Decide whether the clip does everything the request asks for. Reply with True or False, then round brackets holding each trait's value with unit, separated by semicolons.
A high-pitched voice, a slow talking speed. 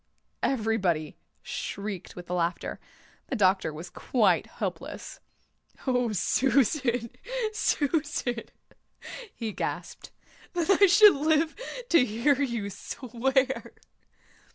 True (245 Hz; 90 wpm)